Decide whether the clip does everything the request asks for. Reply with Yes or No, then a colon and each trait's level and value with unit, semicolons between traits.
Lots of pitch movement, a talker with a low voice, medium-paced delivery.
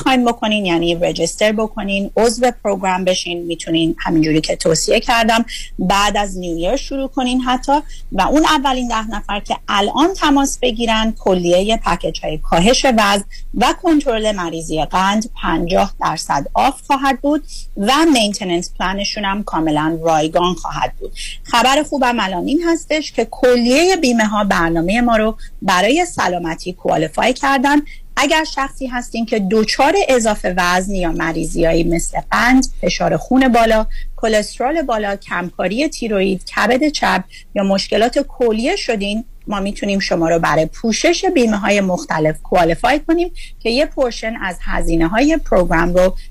No: wide, 6.2 semitones; high, 215 Hz; average, 140 wpm